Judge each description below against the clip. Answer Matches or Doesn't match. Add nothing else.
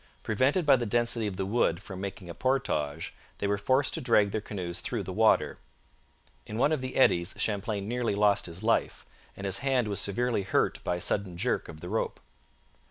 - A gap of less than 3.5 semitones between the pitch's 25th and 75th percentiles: Doesn't match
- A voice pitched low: Matches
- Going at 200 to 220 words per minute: Matches